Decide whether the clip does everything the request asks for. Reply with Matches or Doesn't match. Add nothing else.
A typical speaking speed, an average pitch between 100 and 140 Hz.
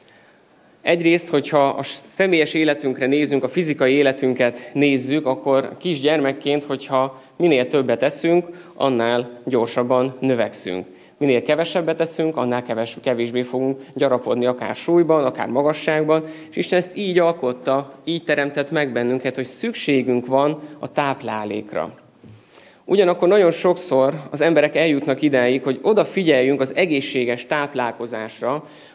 Matches